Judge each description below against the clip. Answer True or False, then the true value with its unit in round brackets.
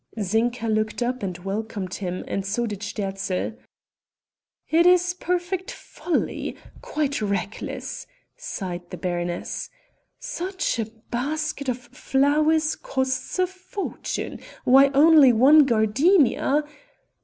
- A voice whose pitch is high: True (255 Hz)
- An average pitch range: False (7.2 semitones)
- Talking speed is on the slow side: True (110 wpm)